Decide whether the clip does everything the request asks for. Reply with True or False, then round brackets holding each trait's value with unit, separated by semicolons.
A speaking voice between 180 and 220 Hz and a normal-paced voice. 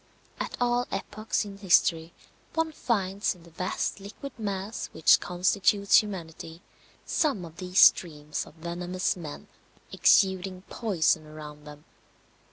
False (185 Hz; 125 wpm)